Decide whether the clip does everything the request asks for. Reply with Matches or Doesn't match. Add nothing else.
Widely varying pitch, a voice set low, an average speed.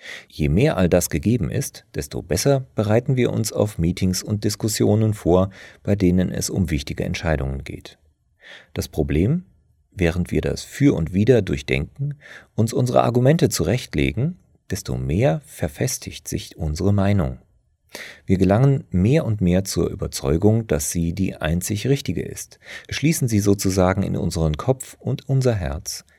Matches